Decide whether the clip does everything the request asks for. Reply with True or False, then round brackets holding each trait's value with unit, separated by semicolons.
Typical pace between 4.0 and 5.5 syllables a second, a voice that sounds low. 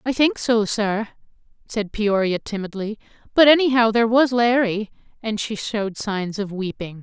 False (4.7 syllables/s; 220 Hz)